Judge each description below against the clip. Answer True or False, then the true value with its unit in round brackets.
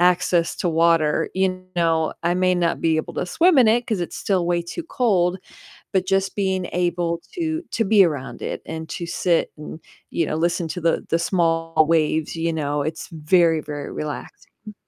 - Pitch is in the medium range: True (170 Hz)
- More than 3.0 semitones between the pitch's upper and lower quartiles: False (2.5 semitones)